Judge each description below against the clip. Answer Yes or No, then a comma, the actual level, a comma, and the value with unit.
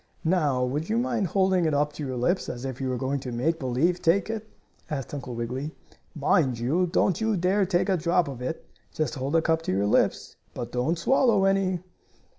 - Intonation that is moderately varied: No, wide, 6.0 semitones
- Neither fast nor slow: No, fast, 215 wpm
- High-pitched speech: No, medium, 160 Hz